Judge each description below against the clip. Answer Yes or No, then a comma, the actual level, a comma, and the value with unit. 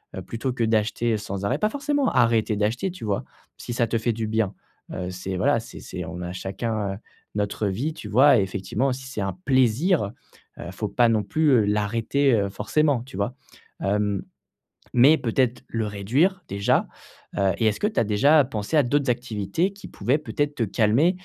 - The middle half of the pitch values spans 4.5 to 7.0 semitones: Yes, average, 5.0 semitones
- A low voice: Yes, low, 115 Hz